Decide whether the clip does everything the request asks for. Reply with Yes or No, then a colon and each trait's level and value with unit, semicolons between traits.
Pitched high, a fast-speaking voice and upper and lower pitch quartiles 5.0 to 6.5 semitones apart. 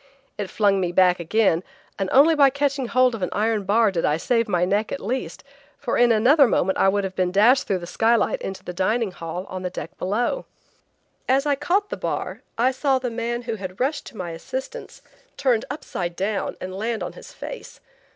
Yes: high, 220 Hz; fast, 210 wpm; wide, 5.5 semitones